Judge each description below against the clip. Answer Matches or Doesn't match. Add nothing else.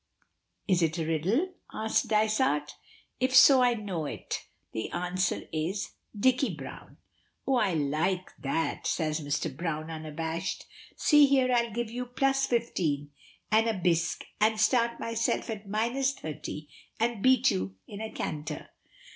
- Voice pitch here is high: Matches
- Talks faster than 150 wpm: Doesn't match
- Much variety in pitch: Matches